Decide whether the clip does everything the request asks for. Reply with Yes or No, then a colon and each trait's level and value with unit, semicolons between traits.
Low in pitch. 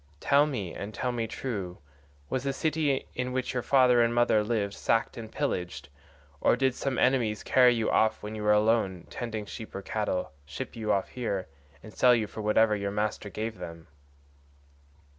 Yes: low, 110 Hz